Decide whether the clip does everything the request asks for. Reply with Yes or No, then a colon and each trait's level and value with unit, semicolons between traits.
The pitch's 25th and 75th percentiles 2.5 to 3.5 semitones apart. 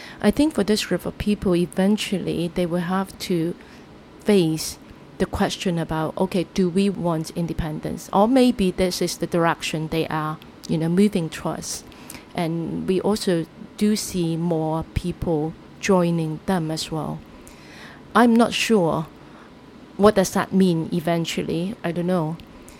Yes: average, 3.0 semitones